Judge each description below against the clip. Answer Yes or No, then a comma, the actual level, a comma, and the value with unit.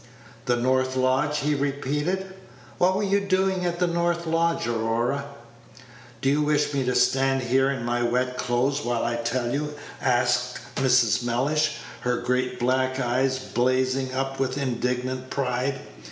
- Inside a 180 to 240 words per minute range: No, average, 155 wpm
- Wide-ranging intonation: No, average, 2.8 semitones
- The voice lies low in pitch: Yes, low, 130 Hz